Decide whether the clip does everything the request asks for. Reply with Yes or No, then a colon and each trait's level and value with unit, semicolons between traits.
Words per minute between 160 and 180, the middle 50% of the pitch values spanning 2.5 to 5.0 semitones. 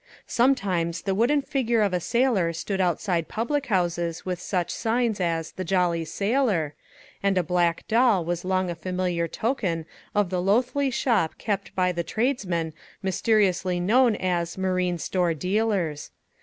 No: average, 150 wpm; average, 4.4 semitones